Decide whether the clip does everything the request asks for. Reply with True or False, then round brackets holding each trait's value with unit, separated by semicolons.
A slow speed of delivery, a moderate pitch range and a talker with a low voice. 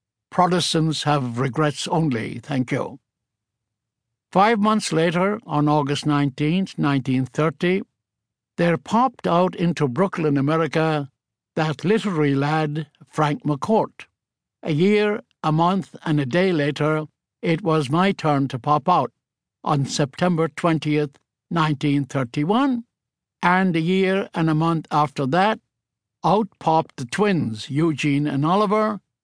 False (125 wpm; 4.3 semitones; 155 Hz)